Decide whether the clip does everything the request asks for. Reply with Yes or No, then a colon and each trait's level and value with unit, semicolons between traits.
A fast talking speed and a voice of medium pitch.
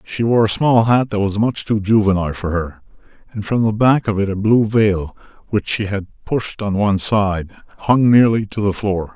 No: fast, 215 wpm; low, 105 Hz